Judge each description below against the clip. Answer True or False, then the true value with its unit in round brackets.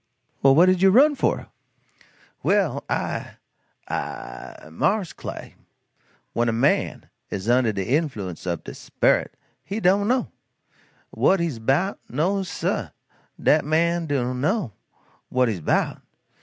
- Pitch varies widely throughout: True (8.0 semitones)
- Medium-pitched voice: True (150 Hz)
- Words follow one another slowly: True (130 wpm)